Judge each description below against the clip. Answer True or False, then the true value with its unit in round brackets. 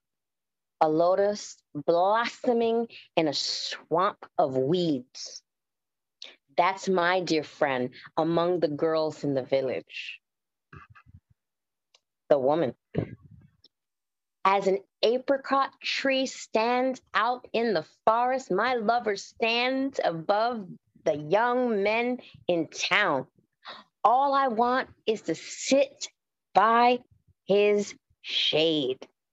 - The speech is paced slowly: True (95 wpm)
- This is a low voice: False (210 Hz)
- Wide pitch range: True (6.6 semitones)